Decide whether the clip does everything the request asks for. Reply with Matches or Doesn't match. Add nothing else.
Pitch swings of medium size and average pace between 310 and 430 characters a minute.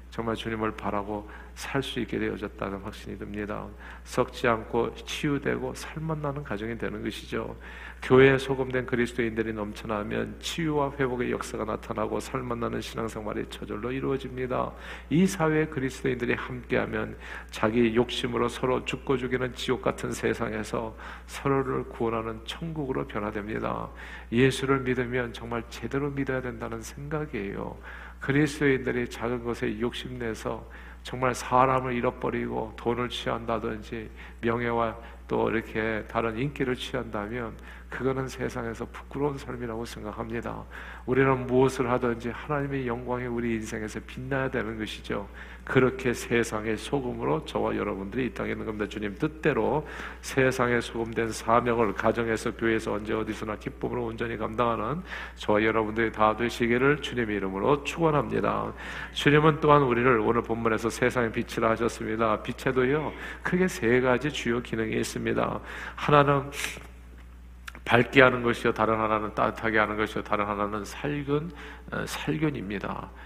Matches